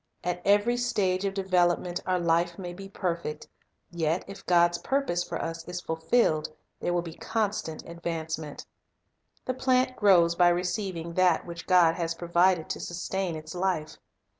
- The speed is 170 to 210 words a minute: No, average, 160 wpm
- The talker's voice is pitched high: No, medium, 175 Hz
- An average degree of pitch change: No, narrow, 2.3 semitones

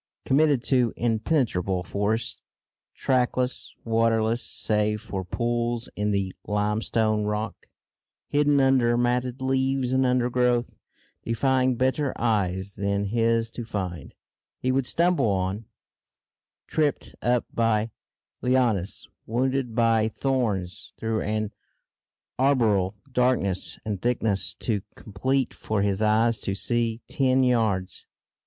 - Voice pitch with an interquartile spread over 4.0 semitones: No, average, 3.3 semitones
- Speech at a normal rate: No, slow, 110 wpm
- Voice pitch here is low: Yes, low, 115 Hz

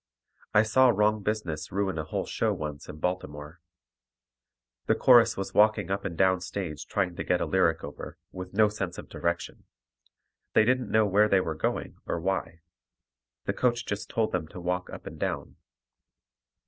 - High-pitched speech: No, very low, 95 Hz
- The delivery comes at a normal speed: Yes, average, 175 wpm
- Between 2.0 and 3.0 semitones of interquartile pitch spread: No, average, 3.9 semitones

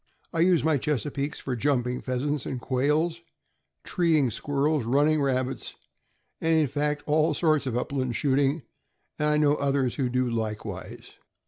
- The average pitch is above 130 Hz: Yes, medium, 140 Hz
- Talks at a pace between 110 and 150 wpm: Yes, average, 145 wpm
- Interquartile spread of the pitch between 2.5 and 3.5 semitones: Yes, average, 2.9 semitones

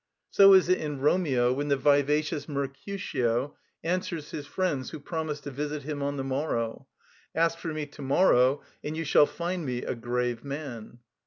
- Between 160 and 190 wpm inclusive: Yes, average, 175 wpm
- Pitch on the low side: No, medium, 145 Hz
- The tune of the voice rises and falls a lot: No, average, 3.1 semitones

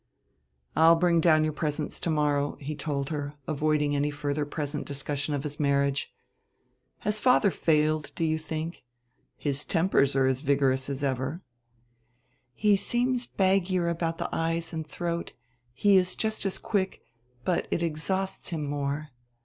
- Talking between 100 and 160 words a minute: Yes, average, 150 wpm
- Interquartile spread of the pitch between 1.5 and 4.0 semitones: Yes, average, 3.1 semitones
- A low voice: No, medium, 155 Hz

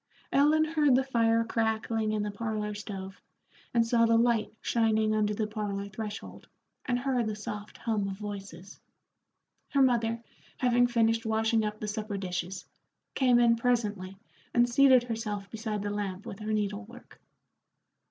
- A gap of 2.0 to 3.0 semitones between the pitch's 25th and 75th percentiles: Yes, narrow, 2.4 semitones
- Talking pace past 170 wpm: No, average, 155 wpm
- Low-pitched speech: No, high, 220 Hz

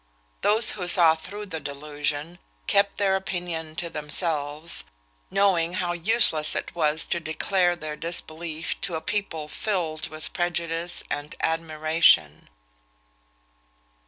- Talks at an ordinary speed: No, slow, 120 wpm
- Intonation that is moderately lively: No, narrow, 2.3 semitones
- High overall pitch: No, medium, 165 Hz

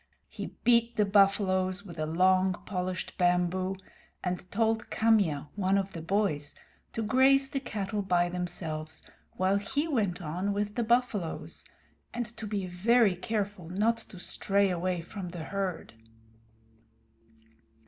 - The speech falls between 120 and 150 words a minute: Yes, average, 140 wpm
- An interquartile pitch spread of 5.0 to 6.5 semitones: No, average, 3.3 semitones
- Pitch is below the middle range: No, high, 195 Hz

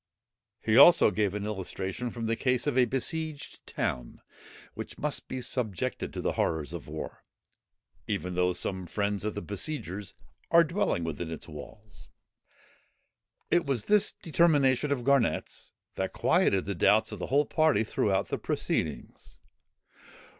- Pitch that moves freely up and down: Yes, wide, 6.8 semitones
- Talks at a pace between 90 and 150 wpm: Yes, average, 145 wpm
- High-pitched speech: No, low, 105 Hz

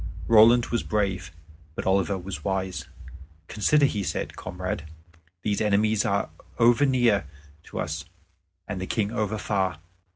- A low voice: Yes, low, 100 Hz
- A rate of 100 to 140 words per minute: Yes, slow, 135 wpm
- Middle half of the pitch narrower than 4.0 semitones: Yes, average, 2.7 semitones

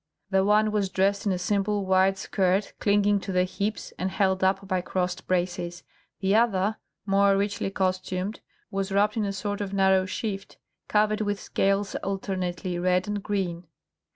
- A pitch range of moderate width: No, narrow, 1.6 semitones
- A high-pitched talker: Yes, high, 195 Hz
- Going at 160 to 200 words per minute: Yes, average, 165 wpm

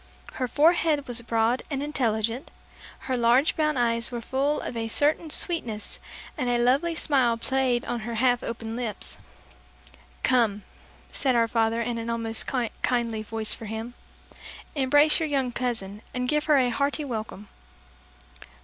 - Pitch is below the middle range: No, high, 245 Hz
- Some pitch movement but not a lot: Yes, average, 3.4 semitones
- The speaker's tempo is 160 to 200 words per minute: No, average, 150 wpm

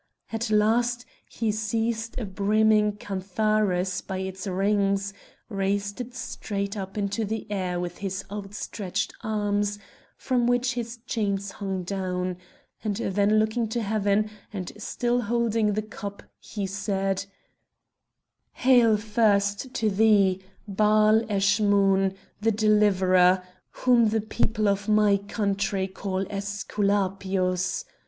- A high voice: Yes, high, 205 Hz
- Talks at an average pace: No, slow, 120 wpm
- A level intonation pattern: Yes, narrow, 1.9 semitones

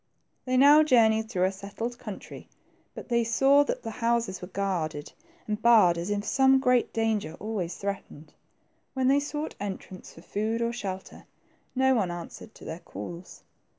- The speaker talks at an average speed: Yes, average, 165 wpm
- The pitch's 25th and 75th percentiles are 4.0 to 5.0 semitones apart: Yes, average, 4.7 semitones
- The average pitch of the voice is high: Yes, high, 220 Hz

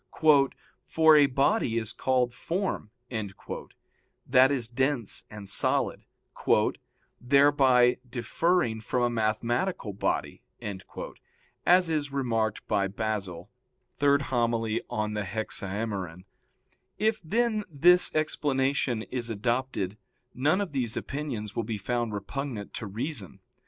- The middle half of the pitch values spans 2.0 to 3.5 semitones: No, average, 4.7 semitones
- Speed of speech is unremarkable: No, slow, 105 wpm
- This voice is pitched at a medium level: No, low, 120 Hz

